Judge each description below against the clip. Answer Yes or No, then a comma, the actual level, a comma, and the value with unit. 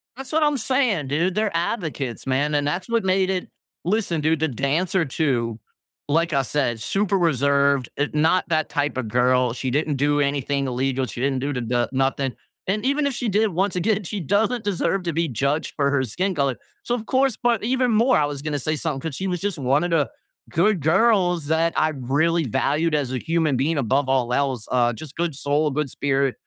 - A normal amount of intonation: No, wide, 5.7 semitones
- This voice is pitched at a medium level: Yes, medium, 155 Hz